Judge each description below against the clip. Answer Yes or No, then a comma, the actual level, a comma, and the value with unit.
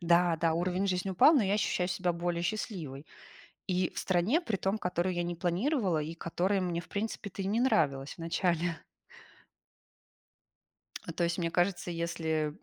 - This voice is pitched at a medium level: Yes, medium, 175 Hz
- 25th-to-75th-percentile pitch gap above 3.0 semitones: No, narrow, 2.4 semitones